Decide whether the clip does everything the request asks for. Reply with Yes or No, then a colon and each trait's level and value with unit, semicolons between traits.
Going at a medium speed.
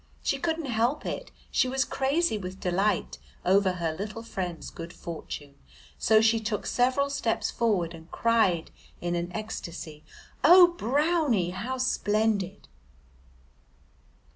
No: slow, 125 wpm